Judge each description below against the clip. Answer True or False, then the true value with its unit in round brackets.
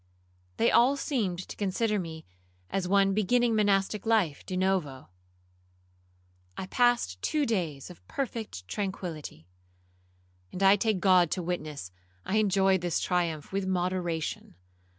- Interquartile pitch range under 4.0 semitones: True (3.6 semitones)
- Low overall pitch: False (190 Hz)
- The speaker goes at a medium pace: False (130 wpm)